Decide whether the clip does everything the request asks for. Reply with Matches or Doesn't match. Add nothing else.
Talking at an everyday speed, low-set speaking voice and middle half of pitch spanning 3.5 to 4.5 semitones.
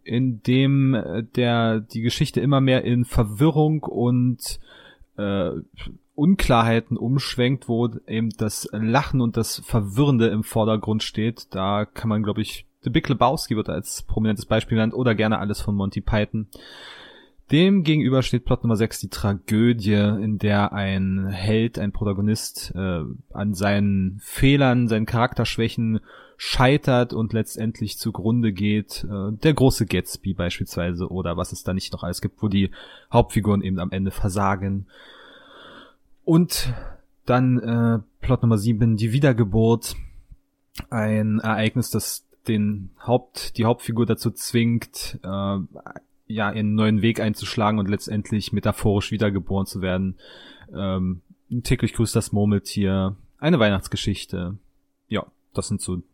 Doesn't match